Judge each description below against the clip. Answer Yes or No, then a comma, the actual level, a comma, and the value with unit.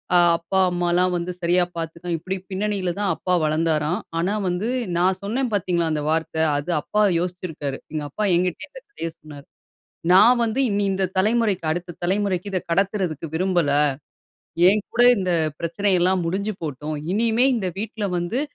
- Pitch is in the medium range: Yes, medium, 180 Hz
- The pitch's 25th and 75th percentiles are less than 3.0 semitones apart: No, average, 3.3 semitones